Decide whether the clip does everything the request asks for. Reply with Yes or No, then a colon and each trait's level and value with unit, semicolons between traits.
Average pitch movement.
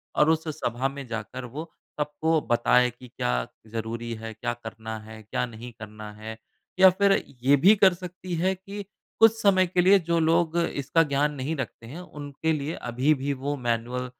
No: wide, 6.1 semitones